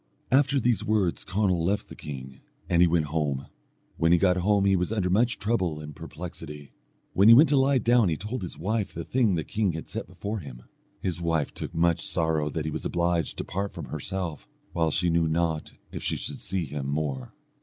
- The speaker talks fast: Yes, fast, 215 wpm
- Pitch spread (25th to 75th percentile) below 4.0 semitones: No, average, 4.5 semitones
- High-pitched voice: No, very low, 85 Hz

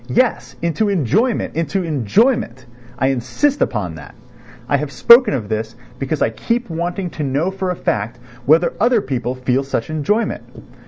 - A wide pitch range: Yes, wide, 8.0 semitones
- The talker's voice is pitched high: No, medium, 155 Hz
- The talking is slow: No, average, 160 wpm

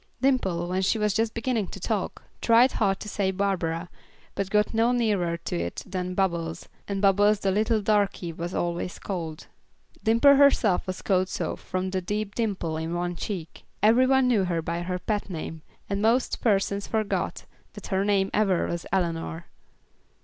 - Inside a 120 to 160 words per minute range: No, average, 175 wpm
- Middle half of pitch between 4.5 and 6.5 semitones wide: No, average, 3.5 semitones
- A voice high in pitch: Yes, high, 195 Hz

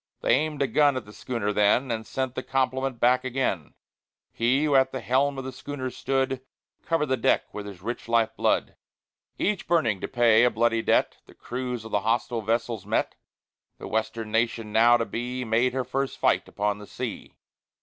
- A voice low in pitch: Yes, low, 120 Hz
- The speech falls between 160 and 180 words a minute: No, average, 200 wpm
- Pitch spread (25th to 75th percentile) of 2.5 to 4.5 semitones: Yes, average, 2.9 semitones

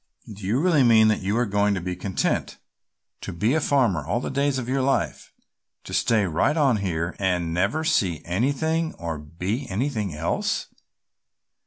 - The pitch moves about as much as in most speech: No, wide, 6.9 semitones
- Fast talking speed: No, average, 175 wpm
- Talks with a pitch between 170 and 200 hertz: No, low, 105 Hz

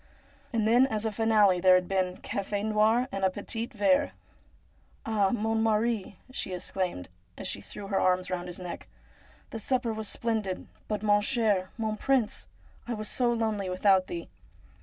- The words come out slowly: No, average, 180 wpm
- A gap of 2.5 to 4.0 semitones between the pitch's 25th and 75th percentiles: Yes, average, 3.0 semitones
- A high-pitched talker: Yes, high, 210 Hz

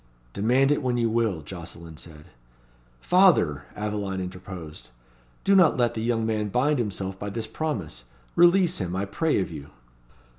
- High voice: No, low, 105 Hz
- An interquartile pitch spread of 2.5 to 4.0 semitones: No, wide, 5.6 semitones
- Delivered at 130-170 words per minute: Yes, average, 155 wpm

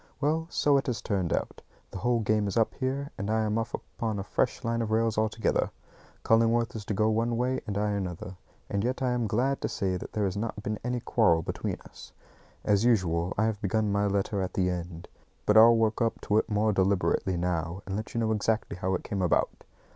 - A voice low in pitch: Yes, low, 110 Hz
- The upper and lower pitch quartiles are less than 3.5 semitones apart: Yes, average, 2.8 semitones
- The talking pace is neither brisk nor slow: No, fast, 230 wpm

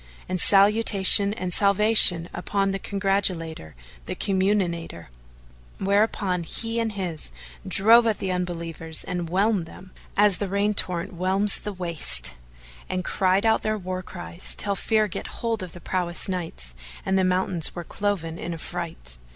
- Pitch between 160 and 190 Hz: Yes, medium, 185 Hz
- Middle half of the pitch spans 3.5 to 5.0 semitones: No, average, 3.1 semitones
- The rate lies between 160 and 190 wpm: No, average, 150 wpm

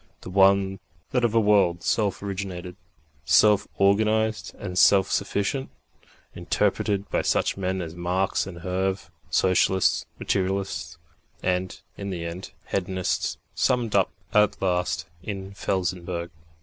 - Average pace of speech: No, slow, 125 wpm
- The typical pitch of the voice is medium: No, very low, 95 Hz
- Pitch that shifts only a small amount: Yes, narrow, 1.8 semitones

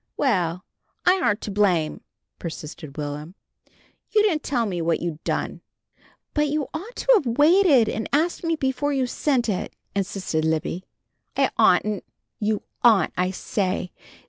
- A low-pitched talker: No, high, 210 Hz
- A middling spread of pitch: No, wide, 8.7 semitones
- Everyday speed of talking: Yes, average, 145 wpm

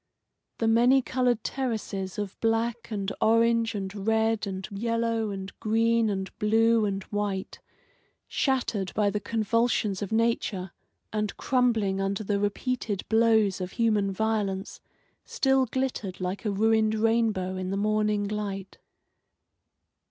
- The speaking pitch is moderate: No, high, 215 Hz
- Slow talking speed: Yes, slow, 130 wpm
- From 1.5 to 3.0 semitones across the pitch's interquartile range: Yes, narrow, 2.6 semitones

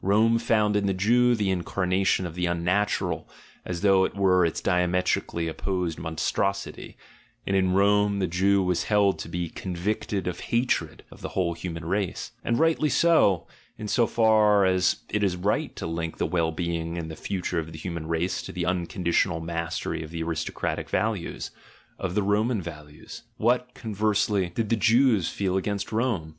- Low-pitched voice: Yes, very low, 95 Hz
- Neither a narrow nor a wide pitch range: Yes, average, 3.5 semitones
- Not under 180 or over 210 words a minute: Yes, average, 185 wpm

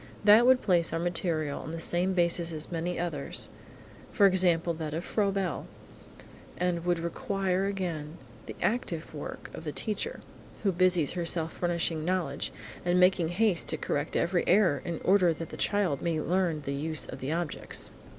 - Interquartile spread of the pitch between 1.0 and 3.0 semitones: Yes, narrow, 2.5 semitones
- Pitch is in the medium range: Yes, medium, 175 Hz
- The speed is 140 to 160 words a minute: No, average, 170 wpm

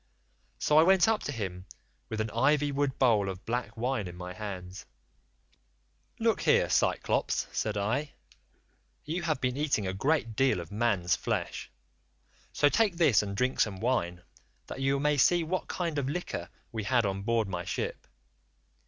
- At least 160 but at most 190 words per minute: Yes, average, 170 wpm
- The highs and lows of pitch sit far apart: Yes, wide, 6.6 semitones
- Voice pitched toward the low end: Yes, low, 120 Hz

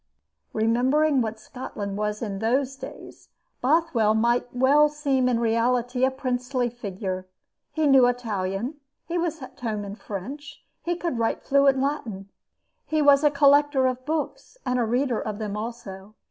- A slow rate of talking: No, average, 155 wpm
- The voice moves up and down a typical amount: Yes, average, 4.2 semitones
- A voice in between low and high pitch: No, very high, 250 Hz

